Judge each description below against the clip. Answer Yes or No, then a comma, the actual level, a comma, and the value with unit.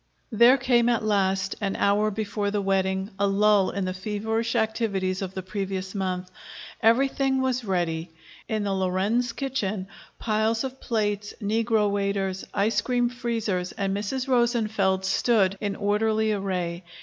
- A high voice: Yes, high, 205 Hz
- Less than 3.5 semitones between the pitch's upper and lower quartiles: Yes, average, 3.0 semitones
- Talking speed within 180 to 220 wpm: No, average, 145 wpm